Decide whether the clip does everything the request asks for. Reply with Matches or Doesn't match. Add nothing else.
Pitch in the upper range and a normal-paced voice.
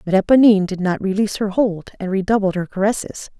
Matches